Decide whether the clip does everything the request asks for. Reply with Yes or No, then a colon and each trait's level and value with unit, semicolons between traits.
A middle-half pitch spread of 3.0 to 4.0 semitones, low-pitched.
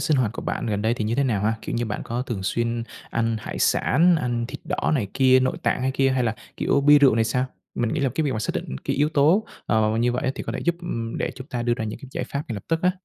Yes: average, 3.6 semitones; low, 125 Hz